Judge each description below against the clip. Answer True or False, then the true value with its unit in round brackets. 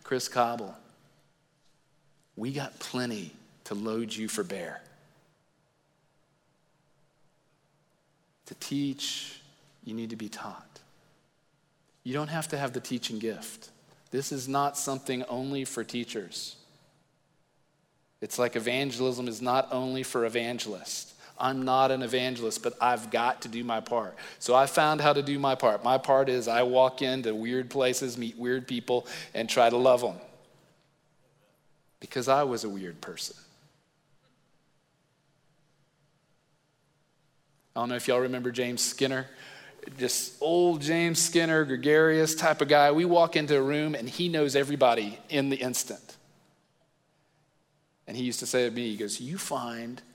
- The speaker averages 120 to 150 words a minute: True (145 wpm)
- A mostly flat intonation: False (3.7 semitones)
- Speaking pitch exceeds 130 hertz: True (140 Hz)